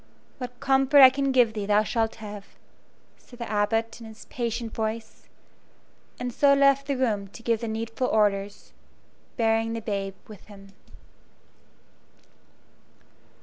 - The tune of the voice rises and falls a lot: No, average, 2.8 semitones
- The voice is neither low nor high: No, high, 225 Hz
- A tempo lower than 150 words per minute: Yes, average, 140 wpm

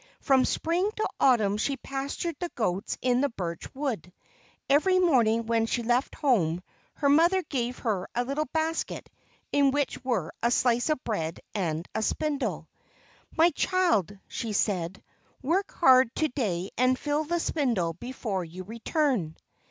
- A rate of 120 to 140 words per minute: No, average, 150 wpm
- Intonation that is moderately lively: No, wide, 6.3 semitones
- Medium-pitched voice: No, very high, 250 Hz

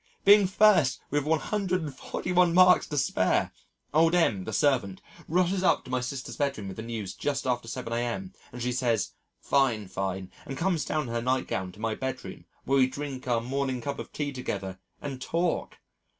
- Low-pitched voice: Yes, low, 130 Hz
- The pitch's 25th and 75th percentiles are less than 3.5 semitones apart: No, average, 5.1 semitones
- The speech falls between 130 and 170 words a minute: No, average, 180 wpm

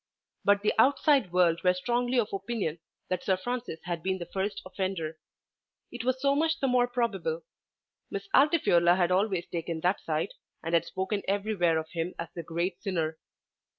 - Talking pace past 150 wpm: Yes, average, 175 wpm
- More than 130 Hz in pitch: Yes, high, 190 Hz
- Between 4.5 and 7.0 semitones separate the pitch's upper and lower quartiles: Yes, wide, 5.4 semitones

